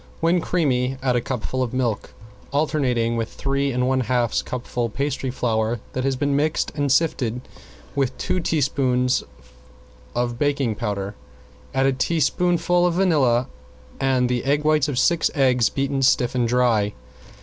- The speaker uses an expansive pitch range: No, average, 2.8 semitones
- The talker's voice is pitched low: Yes, low, 130 Hz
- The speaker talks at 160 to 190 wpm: No, average, 150 wpm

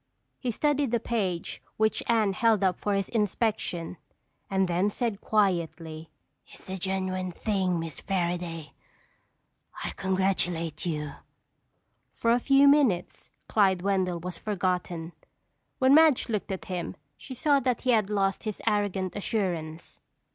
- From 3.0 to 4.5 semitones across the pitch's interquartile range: Yes, average, 3.8 semitones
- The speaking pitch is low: No, high, 190 Hz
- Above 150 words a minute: No, slow, 135 wpm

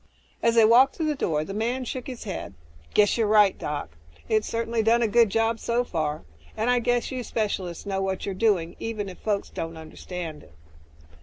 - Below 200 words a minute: No, fast, 205 wpm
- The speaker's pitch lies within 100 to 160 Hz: No, high, 215 Hz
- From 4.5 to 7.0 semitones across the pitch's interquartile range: No, average, 3.8 semitones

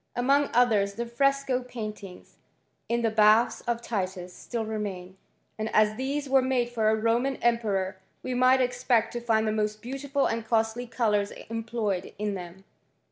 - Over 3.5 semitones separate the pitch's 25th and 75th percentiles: No, average, 2.7 semitones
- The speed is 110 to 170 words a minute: Yes, average, 145 wpm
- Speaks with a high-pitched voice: Yes, high, 230 Hz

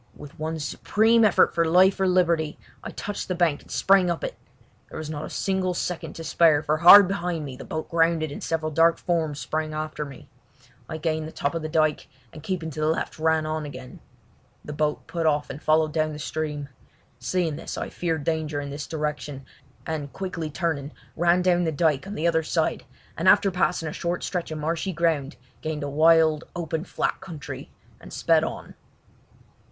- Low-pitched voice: No, medium, 160 Hz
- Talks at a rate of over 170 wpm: Yes, average, 200 wpm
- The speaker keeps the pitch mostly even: Yes, narrow, 2.1 semitones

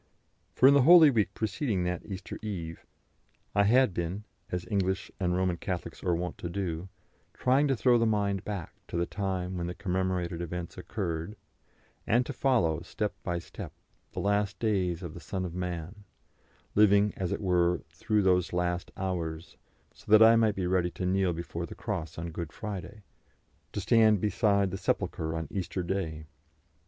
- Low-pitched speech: Yes, very low, 95 Hz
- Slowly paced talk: No, average, 175 wpm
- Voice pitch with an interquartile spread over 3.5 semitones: No, average, 3.2 semitones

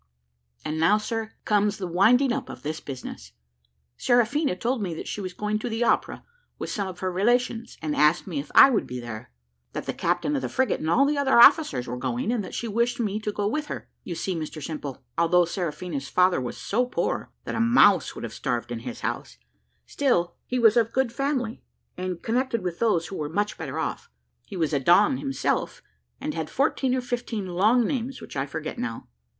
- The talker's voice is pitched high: Yes, high, 205 Hz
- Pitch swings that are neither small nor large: No, wide, 6.3 semitones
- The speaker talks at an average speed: No, fast, 215 wpm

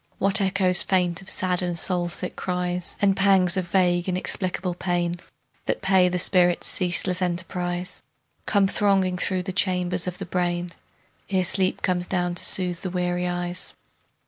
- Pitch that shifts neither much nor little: No, narrow, 1.0 semitones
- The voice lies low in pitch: No, medium, 180 Hz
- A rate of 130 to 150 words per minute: No, average, 160 wpm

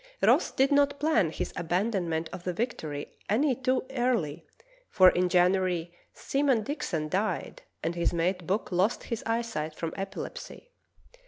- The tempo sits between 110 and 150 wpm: Yes, average, 145 wpm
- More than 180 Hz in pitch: Yes, high, 190 Hz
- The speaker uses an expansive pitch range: Yes, wide, 6.0 semitones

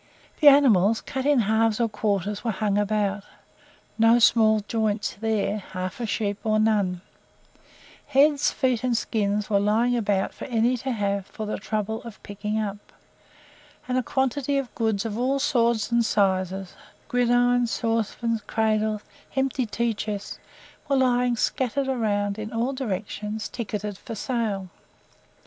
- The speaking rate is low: No, average, 150 wpm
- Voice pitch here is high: Yes, high, 220 Hz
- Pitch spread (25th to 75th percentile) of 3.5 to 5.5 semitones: No, average, 2.8 semitones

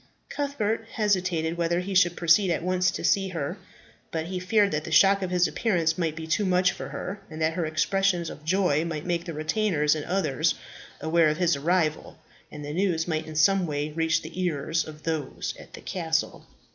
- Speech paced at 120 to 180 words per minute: No, fast, 205 wpm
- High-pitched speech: No, medium, 170 Hz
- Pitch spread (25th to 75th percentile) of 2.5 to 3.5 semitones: Yes, average, 2.8 semitones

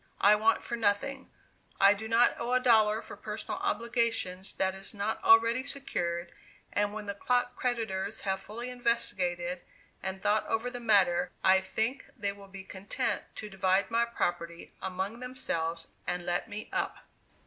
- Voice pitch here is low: No, high, 205 Hz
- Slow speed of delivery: No, average, 160 wpm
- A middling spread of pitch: Yes, average, 3.7 semitones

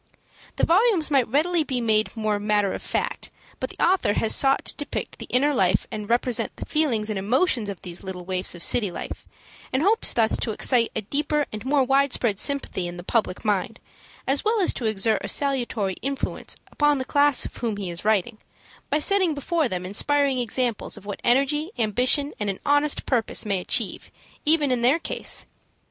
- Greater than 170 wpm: Yes, average, 195 wpm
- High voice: Yes, high, 245 Hz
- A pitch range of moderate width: No, wide, 5.7 semitones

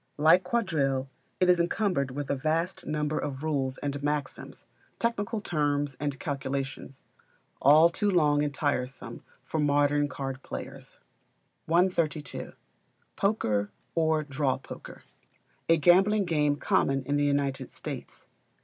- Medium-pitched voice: Yes, medium, 145 Hz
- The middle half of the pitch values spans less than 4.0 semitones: Yes, average, 3.4 semitones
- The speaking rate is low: Yes, slow, 125 wpm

